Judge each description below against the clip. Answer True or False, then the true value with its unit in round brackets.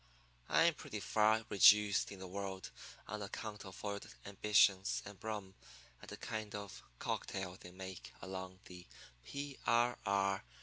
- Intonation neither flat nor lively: False (2.0 semitones)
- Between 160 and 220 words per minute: False (145 wpm)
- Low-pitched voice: True (100 Hz)